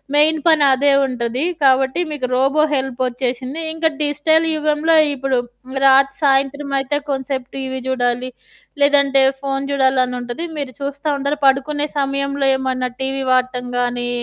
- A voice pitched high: Yes, very high, 270 Hz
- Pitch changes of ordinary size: No, narrow, 1.9 semitones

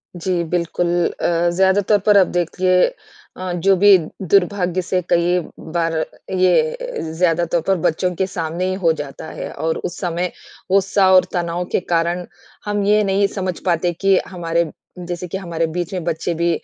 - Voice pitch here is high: No, medium, 180 Hz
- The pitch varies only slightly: Yes, narrow, 2.0 semitones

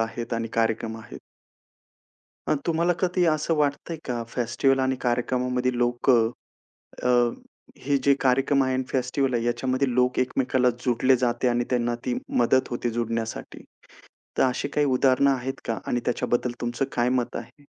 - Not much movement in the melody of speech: Yes, narrow, 1.9 semitones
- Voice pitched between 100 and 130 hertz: Yes, low, 125 Hz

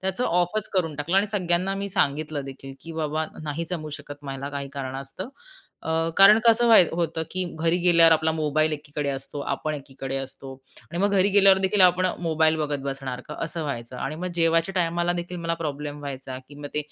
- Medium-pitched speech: Yes, medium, 160 Hz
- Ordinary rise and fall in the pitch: Yes, average, 3.9 semitones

